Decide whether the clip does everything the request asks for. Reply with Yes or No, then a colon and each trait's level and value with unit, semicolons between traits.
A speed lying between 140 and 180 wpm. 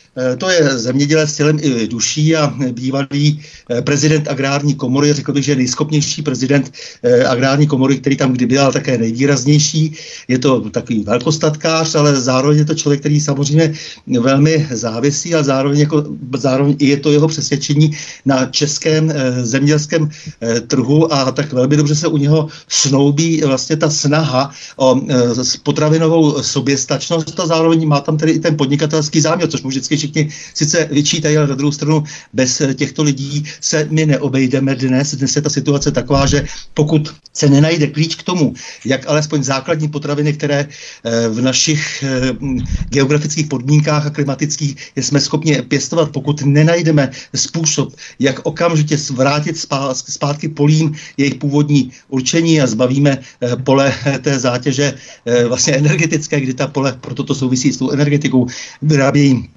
Yes: average, 145 wpm